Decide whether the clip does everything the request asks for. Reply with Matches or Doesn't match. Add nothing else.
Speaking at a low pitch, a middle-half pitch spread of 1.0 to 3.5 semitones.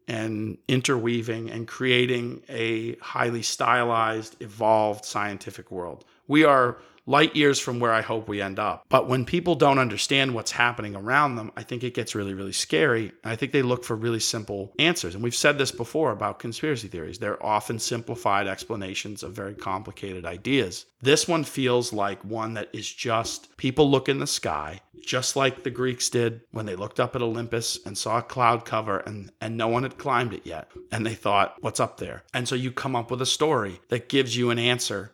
Matches